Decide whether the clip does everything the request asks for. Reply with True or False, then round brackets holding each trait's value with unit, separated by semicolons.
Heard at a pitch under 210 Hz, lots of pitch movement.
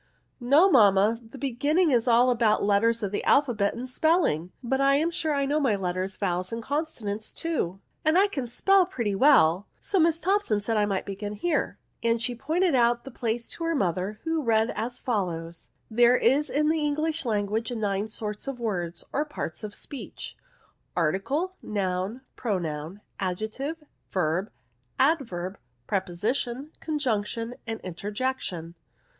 False (230 Hz; 6.0 semitones)